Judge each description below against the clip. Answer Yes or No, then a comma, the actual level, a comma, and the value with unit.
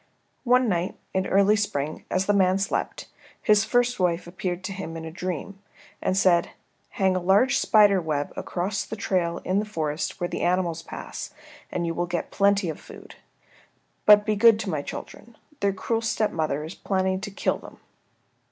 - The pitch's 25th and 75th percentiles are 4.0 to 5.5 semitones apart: No, average, 3.0 semitones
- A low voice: No, high, 190 Hz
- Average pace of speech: Yes, average, 185 wpm